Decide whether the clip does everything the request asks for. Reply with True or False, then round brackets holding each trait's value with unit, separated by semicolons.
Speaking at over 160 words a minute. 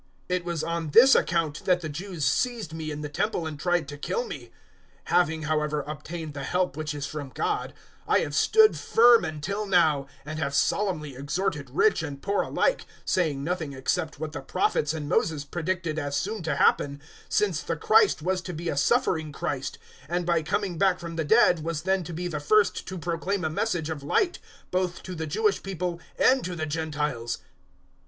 True (200 wpm)